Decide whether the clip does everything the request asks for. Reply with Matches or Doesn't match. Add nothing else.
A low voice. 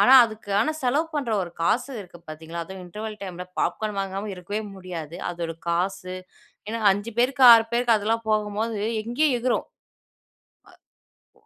Doesn't match